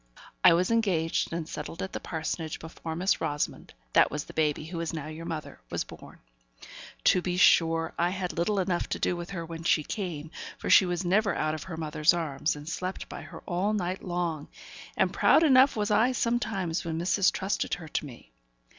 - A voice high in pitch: No, medium, 175 Hz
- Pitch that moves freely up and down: No, average, 2.9 semitones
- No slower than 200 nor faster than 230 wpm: Yes, fast, 205 wpm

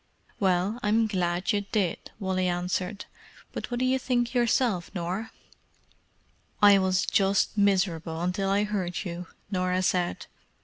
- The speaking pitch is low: No, high, 190 Hz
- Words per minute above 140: No, slow, 135 wpm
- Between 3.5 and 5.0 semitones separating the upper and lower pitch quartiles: No, average, 2.7 semitones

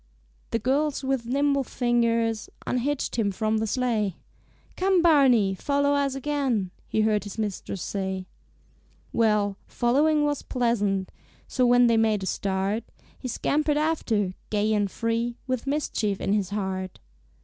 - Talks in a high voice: Yes, high, 230 Hz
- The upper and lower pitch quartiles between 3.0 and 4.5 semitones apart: No, average, 4.9 semitones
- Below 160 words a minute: Yes, average, 140 wpm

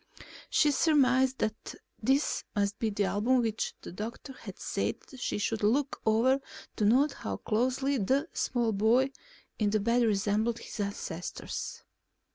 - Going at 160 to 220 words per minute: No, average, 145 wpm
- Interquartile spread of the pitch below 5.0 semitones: Yes, average, 3.8 semitones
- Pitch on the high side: Yes, high, 230 Hz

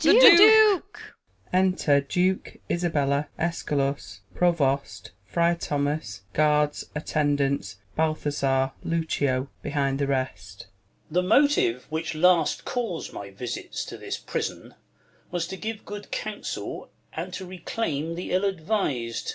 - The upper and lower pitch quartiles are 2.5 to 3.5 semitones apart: No, average, 4.8 semitones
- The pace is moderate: No, slow, 130 wpm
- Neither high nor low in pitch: Yes, medium, 155 Hz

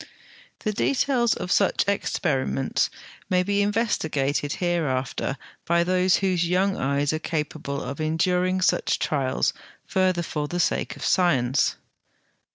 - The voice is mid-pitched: Yes, medium, 175 Hz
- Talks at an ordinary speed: No, slow, 125 wpm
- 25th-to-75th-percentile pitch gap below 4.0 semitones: No, average, 4.5 semitones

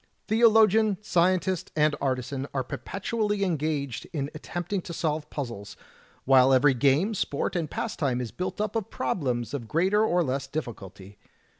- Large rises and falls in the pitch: Yes, wide, 6.2 semitones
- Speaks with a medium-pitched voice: Yes, medium, 150 Hz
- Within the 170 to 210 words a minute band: No, average, 150 wpm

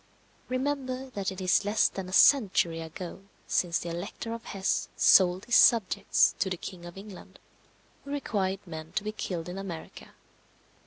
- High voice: Yes, high, 195 Hz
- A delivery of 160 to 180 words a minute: Yes, average, 165 wpm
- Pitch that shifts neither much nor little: Yes, average, 4.1 semitones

